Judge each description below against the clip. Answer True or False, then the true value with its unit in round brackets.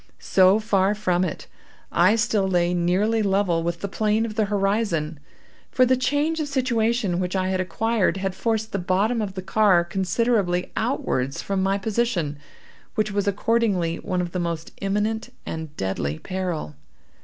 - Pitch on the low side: False (195 Hz)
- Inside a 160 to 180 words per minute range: True (165 wpm)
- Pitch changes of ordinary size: True (3.7 semitones)